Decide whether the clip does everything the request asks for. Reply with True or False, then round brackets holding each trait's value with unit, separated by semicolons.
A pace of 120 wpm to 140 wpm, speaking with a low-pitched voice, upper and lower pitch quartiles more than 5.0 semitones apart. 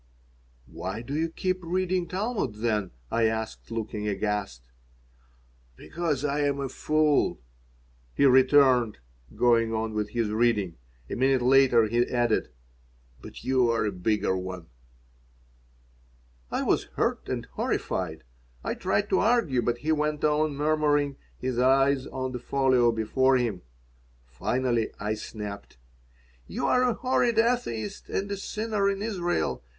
True (135 wpm; 130 Hz; 5.6 semitones)